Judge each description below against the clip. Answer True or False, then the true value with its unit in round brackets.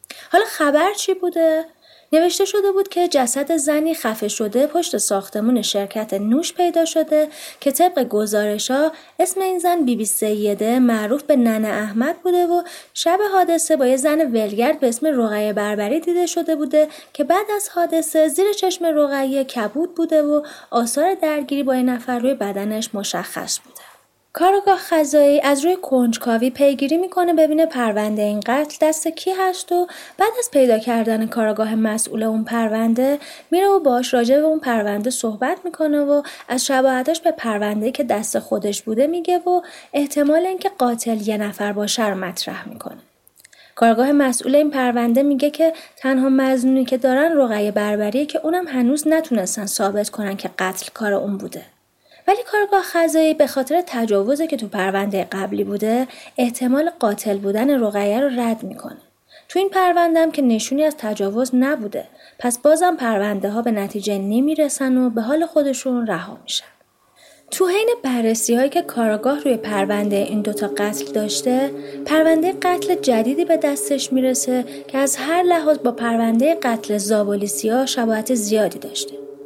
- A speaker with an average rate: False (160 wpm)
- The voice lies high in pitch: True (265 Hz)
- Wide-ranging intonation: True (6.7 semitones)